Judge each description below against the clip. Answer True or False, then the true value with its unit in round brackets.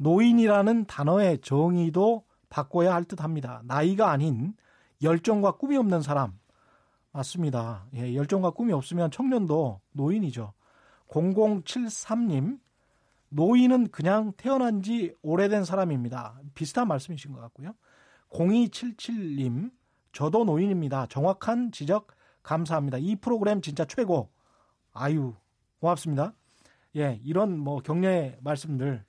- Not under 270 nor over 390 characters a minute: False (260 characters per minute)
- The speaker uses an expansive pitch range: True (6.7 semitones)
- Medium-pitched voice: True (170 Hz)